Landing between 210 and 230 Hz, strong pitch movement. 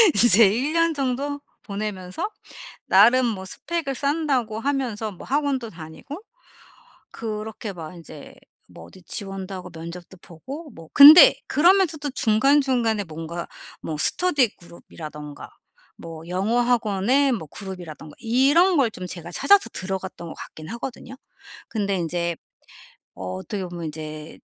Yes: high, 215 Hz; wide, 7.7 semitones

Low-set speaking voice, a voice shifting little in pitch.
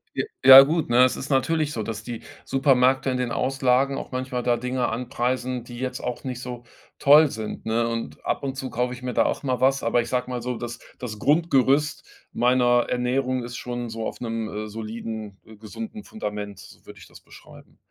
Yes: low, 125 Hz; narrow, 2.2 semitones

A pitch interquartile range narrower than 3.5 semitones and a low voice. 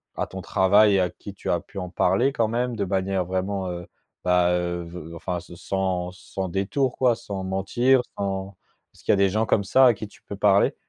Yes: narrow, 2.4 semitones; very low, 95 Hz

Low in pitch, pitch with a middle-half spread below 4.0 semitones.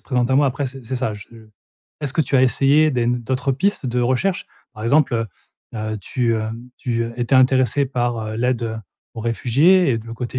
Yes: low, 125 Hz; average, 2.7 semitones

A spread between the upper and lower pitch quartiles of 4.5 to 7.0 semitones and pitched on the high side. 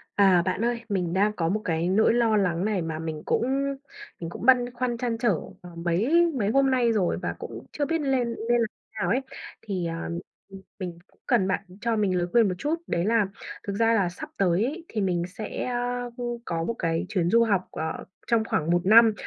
Yes: average, 5.2 semitones; high, 210 Hz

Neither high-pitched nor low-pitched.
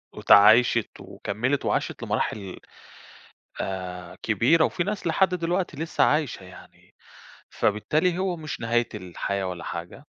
No: low, 125 Hz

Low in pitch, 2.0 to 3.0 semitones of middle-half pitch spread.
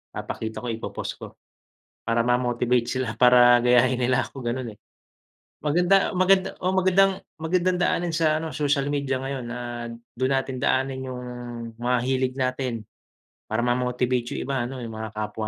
Yes: low, 130 Hz; narrow, 2.6 semitones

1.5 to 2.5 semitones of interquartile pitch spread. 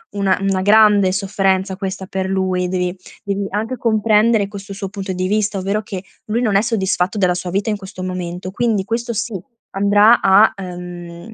Yes: narrow, 2.1 semitones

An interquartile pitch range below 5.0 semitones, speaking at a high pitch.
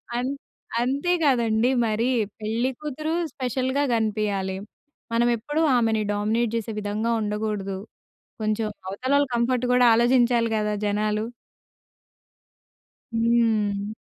Yes: average, 2.8 semitones; high, 225 Hz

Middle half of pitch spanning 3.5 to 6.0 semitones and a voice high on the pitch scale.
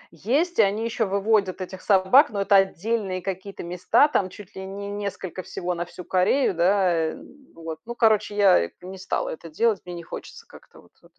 No: average, 2.8 semitones; high, 195 Hz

